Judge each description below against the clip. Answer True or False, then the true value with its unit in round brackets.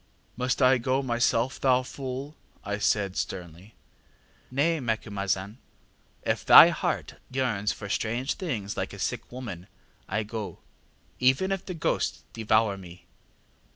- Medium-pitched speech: False (115 Hz)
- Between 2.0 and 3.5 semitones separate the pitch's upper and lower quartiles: False (4.4 semitones)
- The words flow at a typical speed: False (130 wpm)